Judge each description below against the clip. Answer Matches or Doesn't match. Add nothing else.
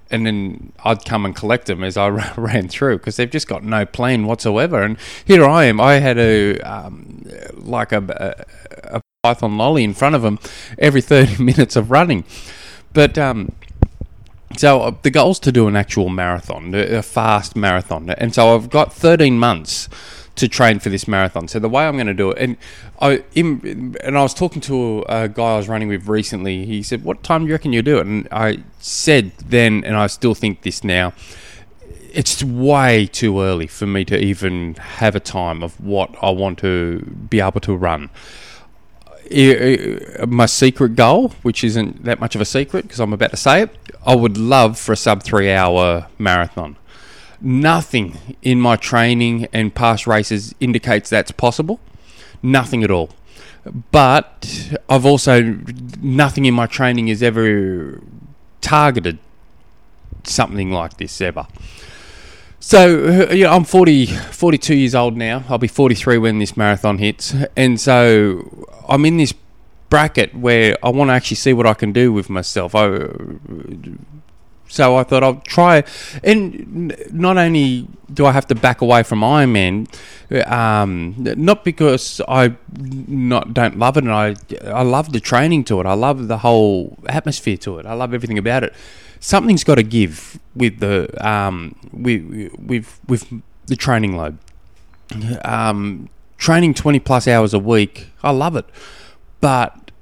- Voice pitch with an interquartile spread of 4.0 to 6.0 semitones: Matches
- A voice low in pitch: Matches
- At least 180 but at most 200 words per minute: Doesn't match